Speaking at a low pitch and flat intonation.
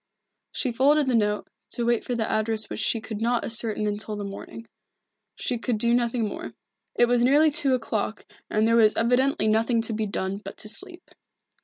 No: high, 230 Hz; narrow, 2.3 semitones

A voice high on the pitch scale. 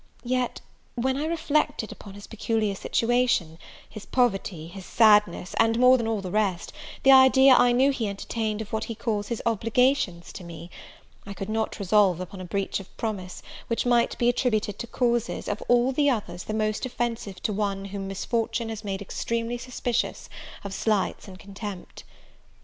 Yes: high, 220 Hz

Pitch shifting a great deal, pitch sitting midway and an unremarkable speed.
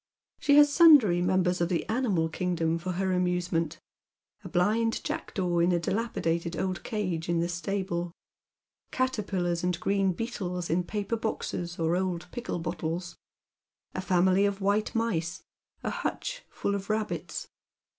No: average, 3.3 semitones; medium, 180 Hz; average, 145 wpm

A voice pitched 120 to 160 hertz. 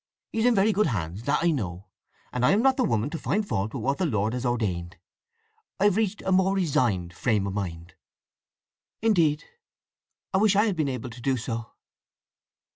Yes: low, 135 Hz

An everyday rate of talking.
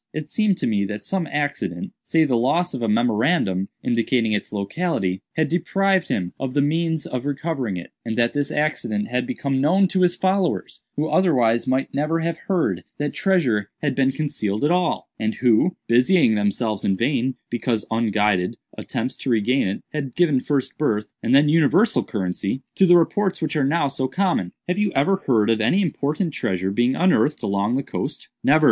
Yes: average, 185 wpm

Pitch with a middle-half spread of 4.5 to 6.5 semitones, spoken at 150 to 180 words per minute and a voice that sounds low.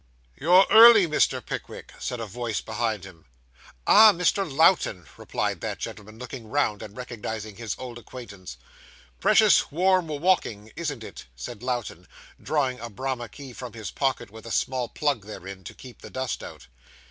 Yes: average, 5.2 semitones; average, 160 wpm; low, 120 Hz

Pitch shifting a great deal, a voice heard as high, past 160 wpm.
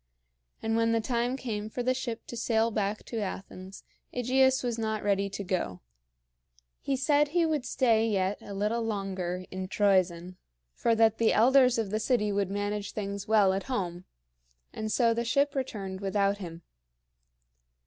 No: average, 3.3 semitones; high, 215 Hz; average, 170 wpm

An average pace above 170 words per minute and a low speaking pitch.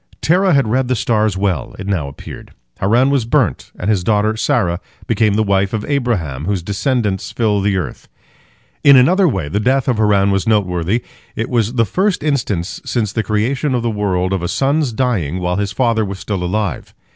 Yes: average, 195 wpm; low, 105 Hz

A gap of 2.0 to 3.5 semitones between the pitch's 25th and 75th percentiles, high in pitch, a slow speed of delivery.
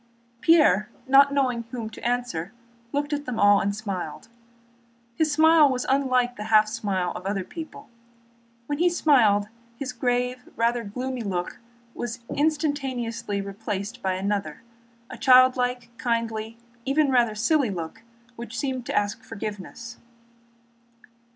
No: average, 3.9 semitones; high, 235 Hz; slow, 130 wpm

